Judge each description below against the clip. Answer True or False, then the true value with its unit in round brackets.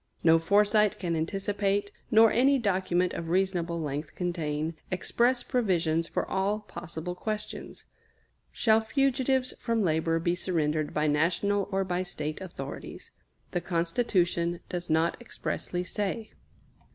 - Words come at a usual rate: False (125 wpm)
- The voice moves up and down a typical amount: True (4.0 semitones)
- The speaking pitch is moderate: True (180 Hz)